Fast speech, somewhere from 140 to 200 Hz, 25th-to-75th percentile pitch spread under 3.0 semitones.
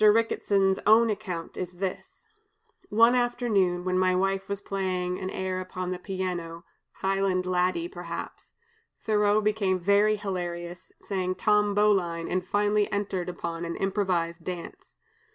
No: slow, 135 wpm; high, 190 Hz; narrow, 2.4 semitones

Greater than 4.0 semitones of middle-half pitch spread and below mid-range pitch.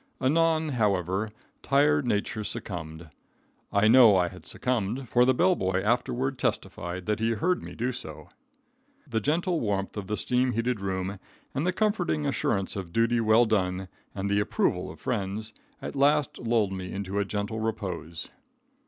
Yes: average, 4.8 semitones; low, 110 Hz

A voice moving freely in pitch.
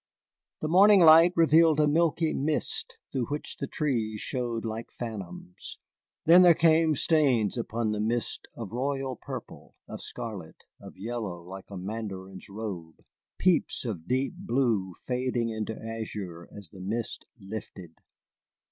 Yes: wide, 6.7 semitones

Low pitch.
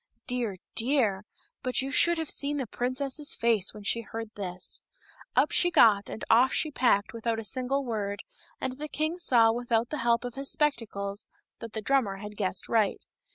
No: high, 235 Hz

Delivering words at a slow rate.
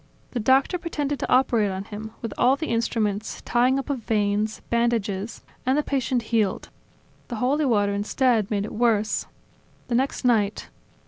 No: average, 170 wpm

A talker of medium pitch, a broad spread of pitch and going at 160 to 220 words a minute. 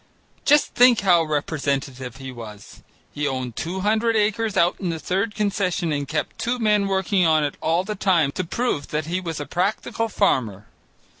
Yes: medium, 175 Hz; wide, 6.1 semitones; average, 180 wpm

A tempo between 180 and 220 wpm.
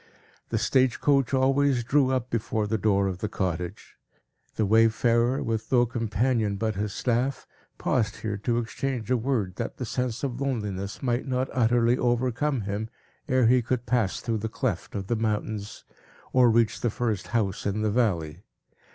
No: average, 170 wpm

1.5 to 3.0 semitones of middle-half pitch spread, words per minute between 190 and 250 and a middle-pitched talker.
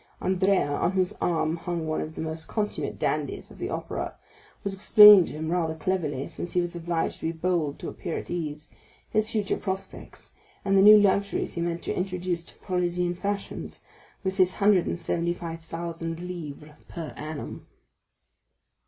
No: narrow, 2.6 semitones; average, 175 wpm; medium, 175 Hz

